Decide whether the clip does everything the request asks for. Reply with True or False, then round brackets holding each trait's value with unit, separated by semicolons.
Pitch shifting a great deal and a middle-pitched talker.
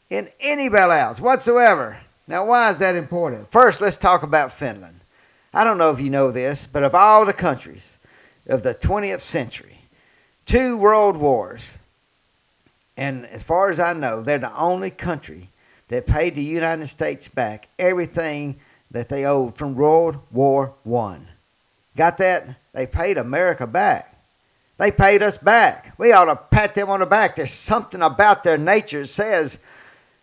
True (6.8 semitones; 155 Hz)